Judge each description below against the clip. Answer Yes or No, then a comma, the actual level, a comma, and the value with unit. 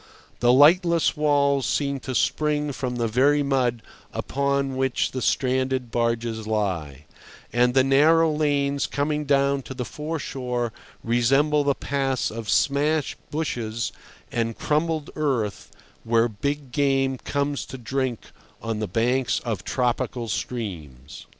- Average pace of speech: No, slow, 130 wpm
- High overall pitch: No, low, 130 Hz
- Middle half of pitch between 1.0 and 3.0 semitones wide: No, average, 3.4 semitones